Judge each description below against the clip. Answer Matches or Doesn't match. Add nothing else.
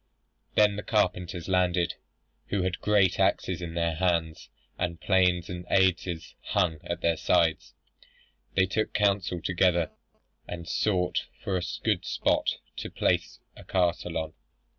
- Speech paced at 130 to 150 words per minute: Matches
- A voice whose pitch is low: Matches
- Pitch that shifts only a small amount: Matches